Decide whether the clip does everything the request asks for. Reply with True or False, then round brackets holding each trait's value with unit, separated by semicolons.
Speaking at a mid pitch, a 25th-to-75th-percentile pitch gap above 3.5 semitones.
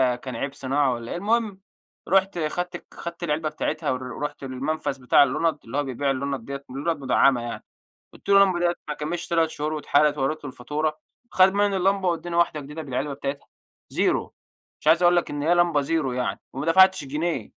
True (150 Hz; 4.0 semitones)